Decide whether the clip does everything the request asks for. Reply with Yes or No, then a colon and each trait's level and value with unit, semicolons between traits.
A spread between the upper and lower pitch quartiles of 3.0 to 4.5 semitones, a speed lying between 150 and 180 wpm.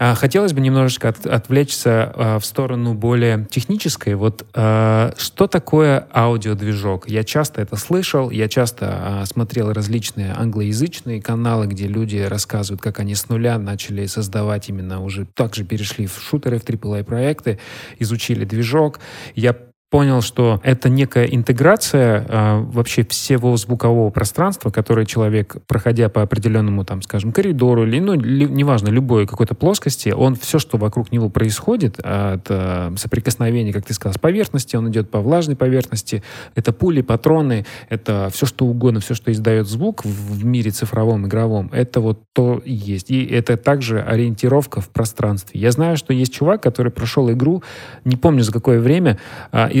Yes: average, 3.3 semitones; fast, 160 wpm